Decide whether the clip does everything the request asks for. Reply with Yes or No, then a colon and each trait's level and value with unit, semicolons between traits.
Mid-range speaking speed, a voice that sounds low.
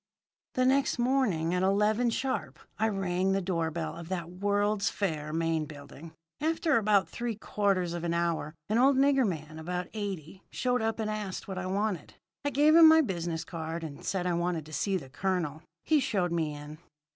No: average, 190 wpm; medium, 185 Hz